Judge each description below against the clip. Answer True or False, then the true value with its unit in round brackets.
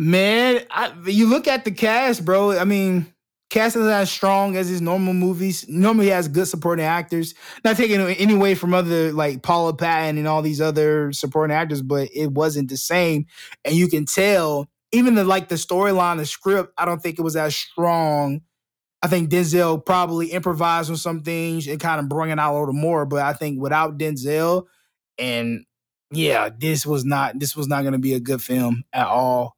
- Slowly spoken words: False (205 wpm)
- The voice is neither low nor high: True (165 Hz)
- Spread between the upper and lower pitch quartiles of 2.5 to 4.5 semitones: True (3.7 semitones)